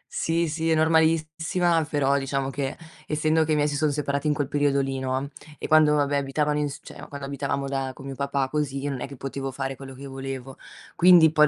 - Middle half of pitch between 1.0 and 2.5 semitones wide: Yes, narrow, 2.2 semitones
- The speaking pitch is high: No, medium, 140 Hz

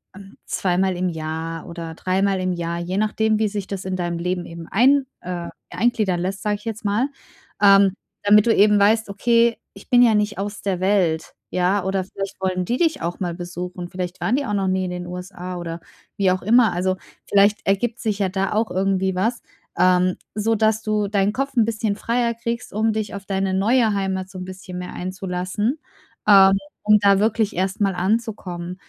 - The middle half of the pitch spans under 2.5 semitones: No, average, 2.8 semitones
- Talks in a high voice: Yes, high, 195 Hz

